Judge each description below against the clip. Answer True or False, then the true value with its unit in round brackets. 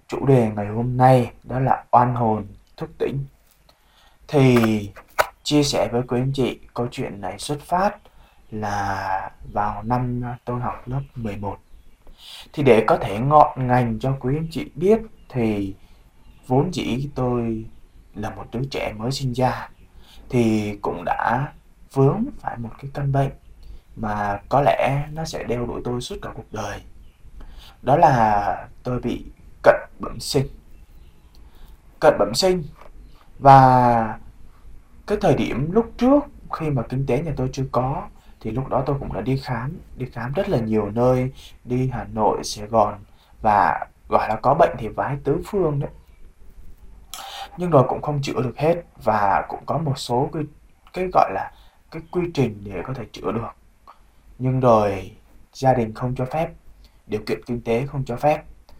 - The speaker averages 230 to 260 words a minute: False (165 wpm)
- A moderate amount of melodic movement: True (4.9 semitones)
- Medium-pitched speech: False (125 Hz)